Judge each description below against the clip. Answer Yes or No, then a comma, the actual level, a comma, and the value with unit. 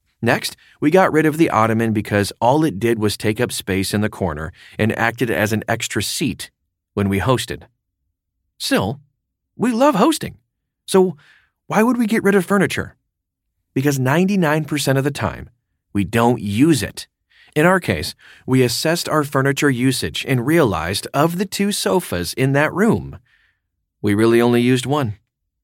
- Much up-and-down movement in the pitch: Yes, wide, 7.1 semitones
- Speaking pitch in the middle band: No, low, 120 Hz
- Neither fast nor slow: Yes, average, 165 wpm